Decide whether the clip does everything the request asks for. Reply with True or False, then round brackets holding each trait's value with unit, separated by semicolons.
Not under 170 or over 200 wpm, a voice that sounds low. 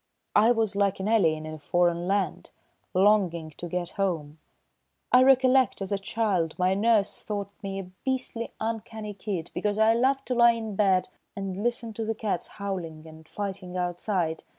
False (175 wpm; 200 Hz)